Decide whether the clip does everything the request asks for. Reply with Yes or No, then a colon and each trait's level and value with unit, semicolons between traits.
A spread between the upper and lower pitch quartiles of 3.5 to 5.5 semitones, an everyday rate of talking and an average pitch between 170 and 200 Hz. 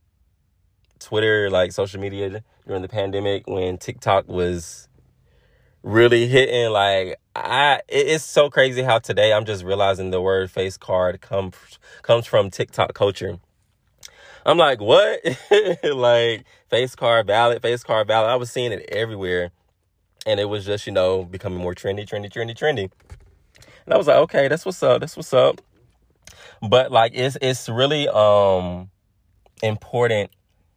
No: average, 3.9 semitones; average, 150 wpm; low, 100 Hz